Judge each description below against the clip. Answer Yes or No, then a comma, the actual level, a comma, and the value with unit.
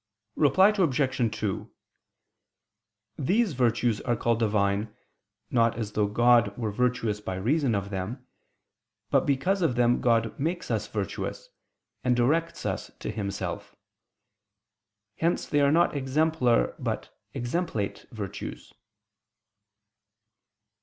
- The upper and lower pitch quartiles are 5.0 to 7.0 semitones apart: Yes, wide, 5.4 semitones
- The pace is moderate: No, slow, 110 wpm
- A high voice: No, low, 120 Hz